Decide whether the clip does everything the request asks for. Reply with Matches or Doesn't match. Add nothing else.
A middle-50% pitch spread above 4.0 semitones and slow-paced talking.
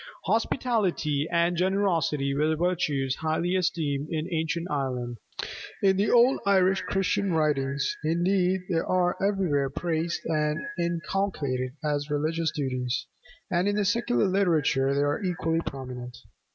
Matches